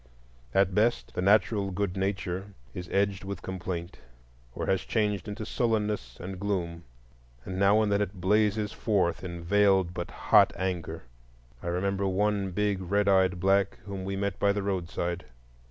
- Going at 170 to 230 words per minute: No, average, 160 wpm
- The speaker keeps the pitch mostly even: Yes, narrow, 1.9 semitones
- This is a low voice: Yes, very low, 95 Hz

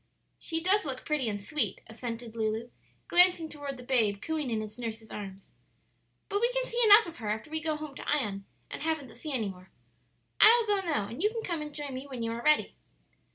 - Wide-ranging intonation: Yes, wide, 6.4 semitones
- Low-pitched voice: No, very high, 275 Hz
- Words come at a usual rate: No, fast, 225 wpm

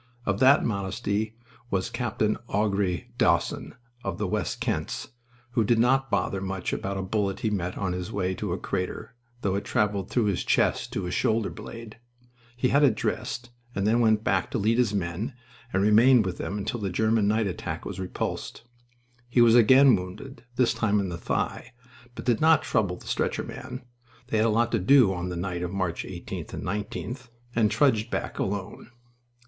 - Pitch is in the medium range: No, low, 105 Hz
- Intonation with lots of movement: No, average, 3.5 semitones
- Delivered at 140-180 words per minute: No, average, 190 wpm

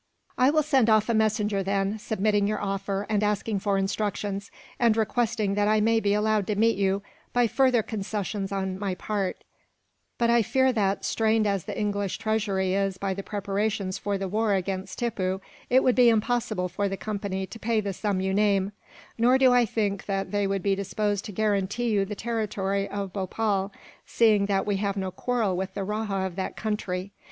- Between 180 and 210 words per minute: Yes, average, 195 wpm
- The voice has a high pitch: Yes, high, 205 Hz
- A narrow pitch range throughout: Yes, narrow, 2.0 semitones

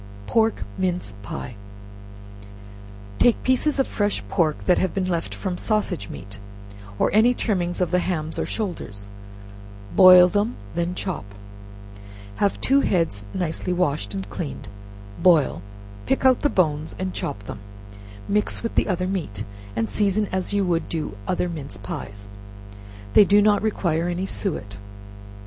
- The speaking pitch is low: No, medium, 180 Hz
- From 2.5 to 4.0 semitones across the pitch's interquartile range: No, average, 5.2 semitones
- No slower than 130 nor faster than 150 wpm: Yes, average, 145 wpm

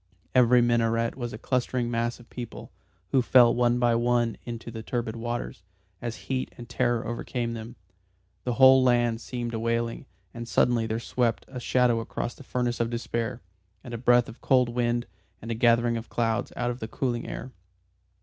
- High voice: No, low, 120 Hz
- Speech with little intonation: Yes, narrow, 1.0 semitones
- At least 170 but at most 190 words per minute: Yes, average, 185 wpm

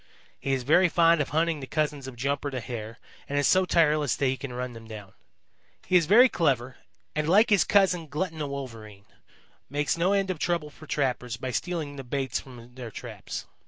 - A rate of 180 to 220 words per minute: Yes, fast, 205 wpm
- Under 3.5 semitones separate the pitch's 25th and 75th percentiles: No, average, 4.8 semitones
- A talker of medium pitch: Yes, medium, 145 Hz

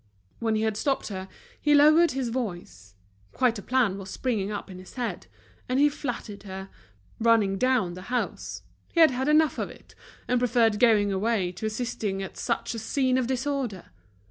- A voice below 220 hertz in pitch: No, high, 230 Hz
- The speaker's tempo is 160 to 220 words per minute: Yes, average, 185 wpm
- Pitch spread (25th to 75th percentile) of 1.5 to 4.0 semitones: No, average, 4.6 semitones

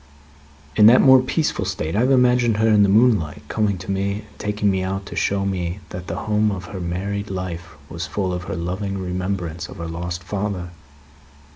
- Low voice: Yes, very low, 95 Hz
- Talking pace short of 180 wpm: No, average, 200 wpm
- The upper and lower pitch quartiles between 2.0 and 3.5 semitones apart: Yes, average, 2.7 semitones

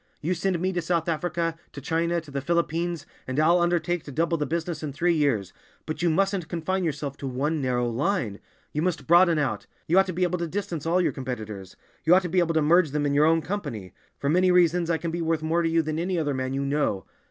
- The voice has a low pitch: No, medium, 165 Hz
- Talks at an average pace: No, fast, 245 wpm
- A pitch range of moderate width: Yes, average, 3.2 semitones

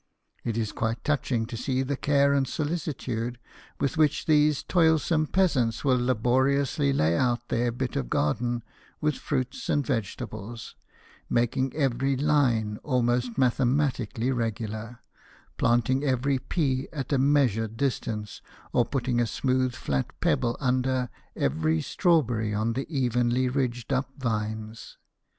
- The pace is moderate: No, slow, 130 wpm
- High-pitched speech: No, low, 125 Hz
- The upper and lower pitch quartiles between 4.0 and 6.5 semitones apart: No, average, 3.1 semitones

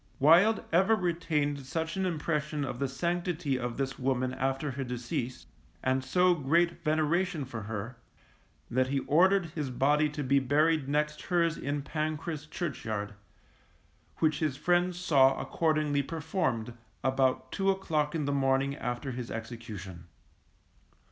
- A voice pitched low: No, medium, 145 Hz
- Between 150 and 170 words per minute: No, average, 140 wpm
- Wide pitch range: No, average, 4.0 semitones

